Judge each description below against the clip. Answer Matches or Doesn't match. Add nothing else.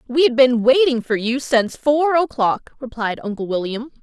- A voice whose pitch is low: Doesn't match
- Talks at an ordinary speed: Matches